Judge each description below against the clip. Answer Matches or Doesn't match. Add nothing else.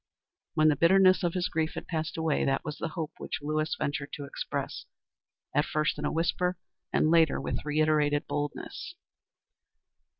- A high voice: Doesn't match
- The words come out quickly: Doesn't match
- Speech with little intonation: Matches